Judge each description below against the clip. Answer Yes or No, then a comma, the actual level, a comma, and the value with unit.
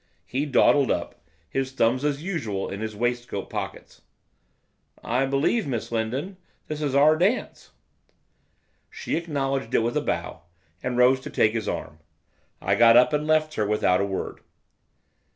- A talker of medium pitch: No, low, 130 Hz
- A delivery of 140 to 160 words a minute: Yes, average, 155 wpm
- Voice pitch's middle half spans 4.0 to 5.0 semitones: Yes, average, 4.7 semitones